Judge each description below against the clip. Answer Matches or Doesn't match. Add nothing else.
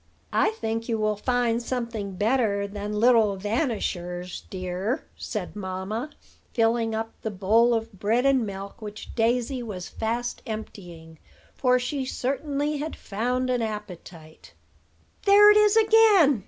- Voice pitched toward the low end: Doesn't match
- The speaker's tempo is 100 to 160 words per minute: Matches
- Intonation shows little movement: Doesn't match